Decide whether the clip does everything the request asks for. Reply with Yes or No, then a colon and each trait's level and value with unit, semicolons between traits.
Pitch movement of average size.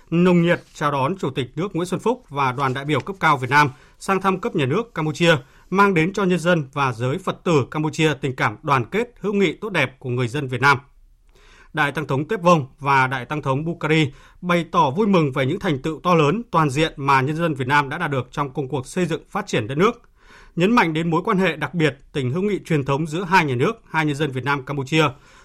Yes: average, 4.4 semitones